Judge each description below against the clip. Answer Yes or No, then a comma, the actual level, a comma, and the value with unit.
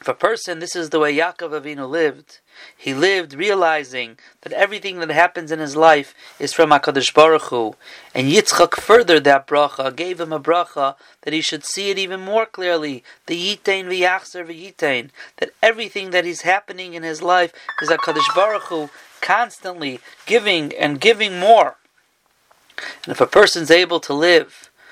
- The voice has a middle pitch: Yes, medium, 170 Hz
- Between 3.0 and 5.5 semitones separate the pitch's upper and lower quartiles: Yes, average, 4.3 semitones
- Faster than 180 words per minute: No, average, 170 wpm